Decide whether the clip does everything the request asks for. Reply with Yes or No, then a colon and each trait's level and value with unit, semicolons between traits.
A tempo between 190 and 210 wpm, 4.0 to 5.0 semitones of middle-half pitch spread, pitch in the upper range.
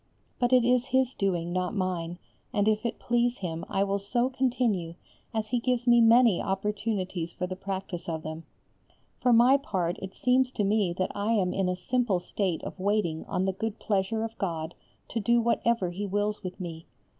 Yes: average, 195 wpm; average, 4.5 semitones; high, 200 Hz